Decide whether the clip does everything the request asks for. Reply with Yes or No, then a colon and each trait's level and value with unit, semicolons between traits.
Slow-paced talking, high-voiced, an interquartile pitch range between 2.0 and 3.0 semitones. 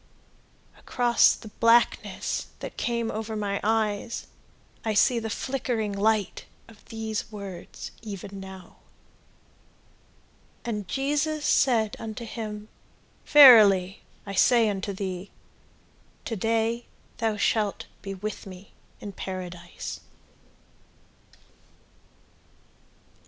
Yes: slow, 95 wpm; high, 215 Hz; narrow, 2.6 semitones